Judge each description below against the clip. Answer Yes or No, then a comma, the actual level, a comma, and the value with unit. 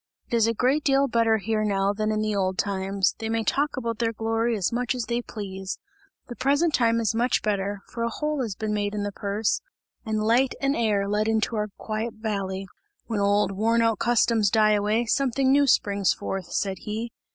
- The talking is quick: Yes, fast, 210 wpm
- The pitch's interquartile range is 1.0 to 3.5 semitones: Yes, narrow, 2.6 semitones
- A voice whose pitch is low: No, high, 220 Hz